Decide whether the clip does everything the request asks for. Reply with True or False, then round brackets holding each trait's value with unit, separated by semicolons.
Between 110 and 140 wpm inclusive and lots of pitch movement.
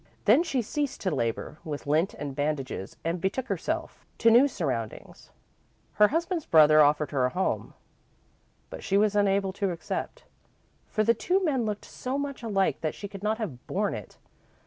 False (175 wpm; 7.7 semitones)